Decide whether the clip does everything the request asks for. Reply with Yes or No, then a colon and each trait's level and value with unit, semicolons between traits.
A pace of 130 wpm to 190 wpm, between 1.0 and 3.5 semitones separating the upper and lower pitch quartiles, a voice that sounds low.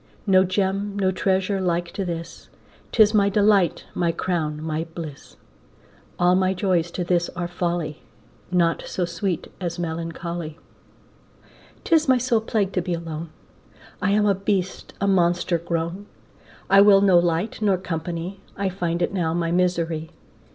No: average, 150 wpm; narrow, 2.6 semitones; medium, 180 Hz